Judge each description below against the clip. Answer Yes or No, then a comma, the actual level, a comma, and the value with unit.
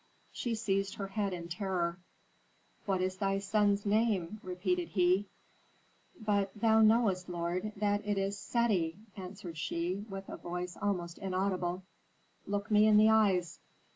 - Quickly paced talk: No, average, 140 wpm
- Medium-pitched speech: No, high, 195 Hz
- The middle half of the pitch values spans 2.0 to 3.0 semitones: Yes, narrow, 2.5 semitones